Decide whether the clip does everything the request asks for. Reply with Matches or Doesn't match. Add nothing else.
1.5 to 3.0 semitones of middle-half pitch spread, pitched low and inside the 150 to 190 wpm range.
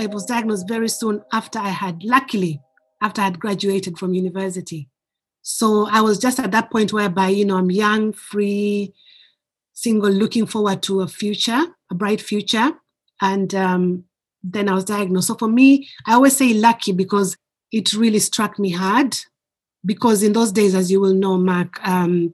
Doesn't match